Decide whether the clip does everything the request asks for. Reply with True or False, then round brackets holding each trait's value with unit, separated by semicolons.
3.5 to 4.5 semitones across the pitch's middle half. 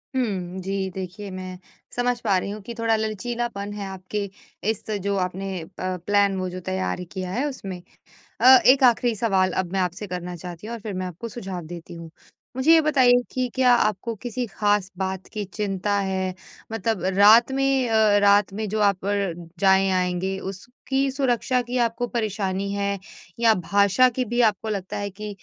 True (3.8 semitones)